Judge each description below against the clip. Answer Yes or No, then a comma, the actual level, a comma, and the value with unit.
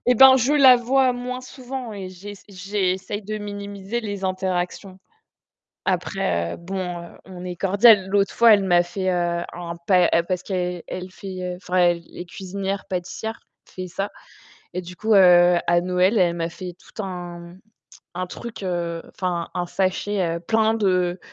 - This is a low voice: No, medium, 185 Hz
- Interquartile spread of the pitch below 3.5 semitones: Yes, narrow, 2.5 semitones